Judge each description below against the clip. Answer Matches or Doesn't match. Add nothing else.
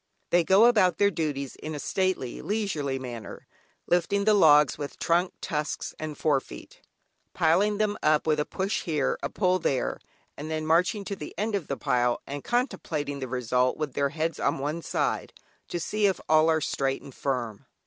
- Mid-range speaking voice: Matches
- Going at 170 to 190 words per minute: Matches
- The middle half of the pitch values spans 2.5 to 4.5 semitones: Doesn't match